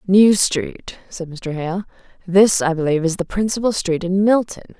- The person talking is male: No, female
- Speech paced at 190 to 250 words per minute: No, average, 175 wpm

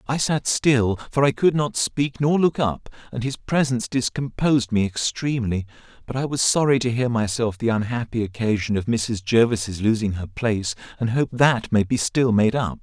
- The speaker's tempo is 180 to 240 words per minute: Yes, average, 190 wpm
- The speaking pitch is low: Yes, low, 120 Hz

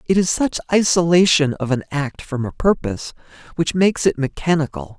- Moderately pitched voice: Yes, medium, 155 Hz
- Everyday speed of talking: Yes, average, 170 wpm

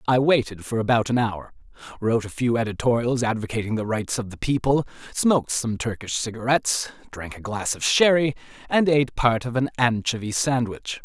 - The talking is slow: No, average, 175 wpm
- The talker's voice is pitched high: No, low, 120 Hz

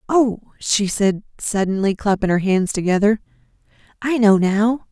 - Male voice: No, female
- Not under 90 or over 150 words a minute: Yes, slow, 135 wpm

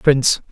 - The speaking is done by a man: Yes, male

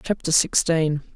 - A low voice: No, medium, 160 Hz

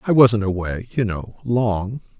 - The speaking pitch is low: Yes, low, 110 Hz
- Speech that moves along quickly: No, average, 165 wpm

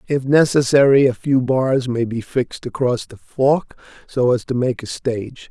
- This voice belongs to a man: Yes, male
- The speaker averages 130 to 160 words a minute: No, average, 185 wpm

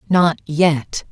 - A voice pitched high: No, medium, 160 Hz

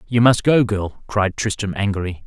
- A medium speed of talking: Yes, average, 185 wpm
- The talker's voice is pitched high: No, low, 105 Hz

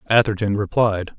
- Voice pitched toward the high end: No, low, 105 Hz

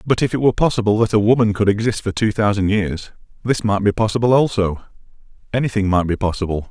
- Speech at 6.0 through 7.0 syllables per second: Yes, 6.5 syllables/s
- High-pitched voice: No, low, 105 Hz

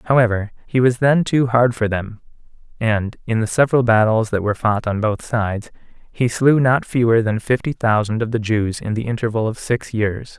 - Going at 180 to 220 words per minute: Yes, average, 200 wpm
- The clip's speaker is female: No, male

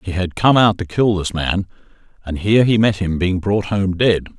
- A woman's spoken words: No, male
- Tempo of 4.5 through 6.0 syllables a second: Yes, 5.0 syllables/s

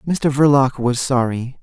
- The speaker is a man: Yes, male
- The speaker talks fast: No, average, 145 wpm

